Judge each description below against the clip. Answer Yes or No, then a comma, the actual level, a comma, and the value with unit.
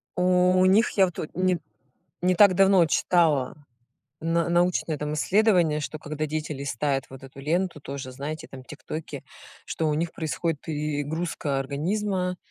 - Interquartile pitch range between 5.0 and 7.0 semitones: No, average, 3.7 semitones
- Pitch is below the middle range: No, medium, 160 Hz